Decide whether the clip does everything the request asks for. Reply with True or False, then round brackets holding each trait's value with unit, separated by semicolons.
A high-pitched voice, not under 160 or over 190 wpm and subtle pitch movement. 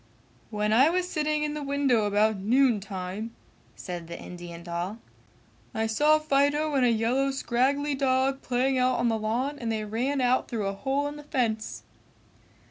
False (250 Hz; 175 wpm; 4.6 semitones)